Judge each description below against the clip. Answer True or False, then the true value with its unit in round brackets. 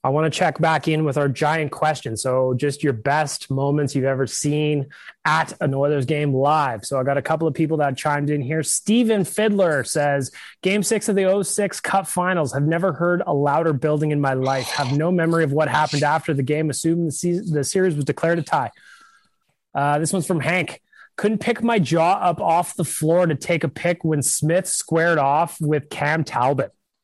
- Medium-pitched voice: True (155 Hz)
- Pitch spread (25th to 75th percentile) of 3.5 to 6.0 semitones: False (3.1 semitones)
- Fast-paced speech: True (210 wpm)